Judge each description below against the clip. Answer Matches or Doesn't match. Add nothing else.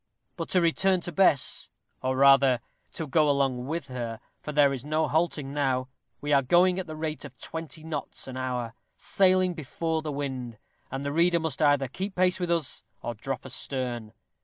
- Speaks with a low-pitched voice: Doesn't match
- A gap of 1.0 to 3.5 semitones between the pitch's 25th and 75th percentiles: Doesn't match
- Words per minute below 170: Doesn't match